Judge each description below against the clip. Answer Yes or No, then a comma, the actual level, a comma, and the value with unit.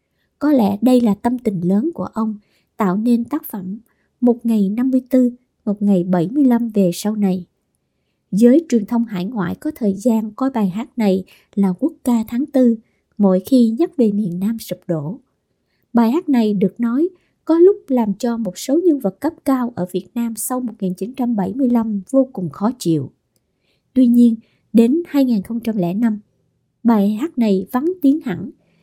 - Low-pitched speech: No, high, 230 Hz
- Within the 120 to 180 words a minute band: Yes, average, 170 wpm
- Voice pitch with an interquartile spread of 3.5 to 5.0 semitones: Yes, average, 4.5 semitones